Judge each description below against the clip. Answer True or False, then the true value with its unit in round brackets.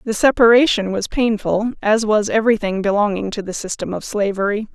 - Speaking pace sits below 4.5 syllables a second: False (5.5 syllables/s)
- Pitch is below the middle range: False (215 Hz)